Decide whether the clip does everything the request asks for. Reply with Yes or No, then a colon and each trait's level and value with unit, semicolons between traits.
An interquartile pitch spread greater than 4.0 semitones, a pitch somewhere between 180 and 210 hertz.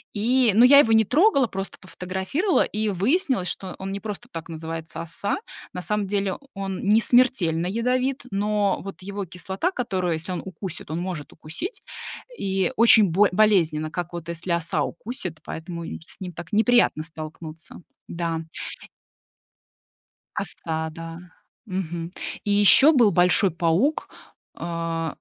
Yes: average, 4.4 semitones; high, 190 Hz